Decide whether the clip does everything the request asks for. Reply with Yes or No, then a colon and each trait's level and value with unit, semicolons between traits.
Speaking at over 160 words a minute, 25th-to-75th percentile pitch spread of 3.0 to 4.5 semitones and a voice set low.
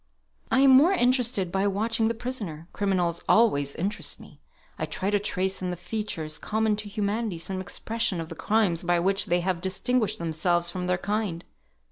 No: average, 180 wpm; average, 4.1 semitones; high, 195 Hz